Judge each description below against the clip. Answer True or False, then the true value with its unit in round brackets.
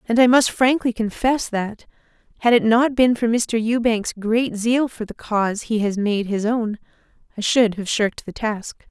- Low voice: False (225 Hz)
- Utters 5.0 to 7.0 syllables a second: False (4.5 syllables/s)